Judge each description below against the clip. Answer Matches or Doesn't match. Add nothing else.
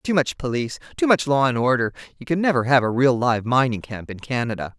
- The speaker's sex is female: Matches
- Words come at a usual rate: Doesn't match